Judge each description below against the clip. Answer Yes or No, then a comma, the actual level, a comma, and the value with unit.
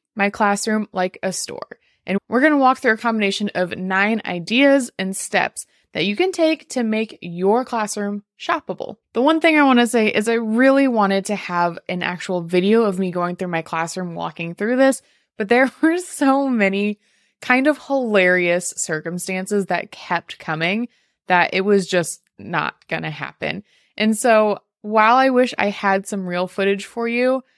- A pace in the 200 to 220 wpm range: No, average, 175 wpm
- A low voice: No, high, 205 Hz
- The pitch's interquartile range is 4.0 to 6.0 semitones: Yes, average, 5.0 semitones